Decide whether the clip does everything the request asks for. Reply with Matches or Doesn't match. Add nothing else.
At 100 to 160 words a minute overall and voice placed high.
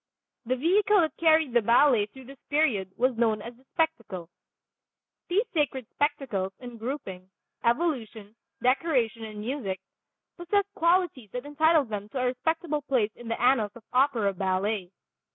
Matches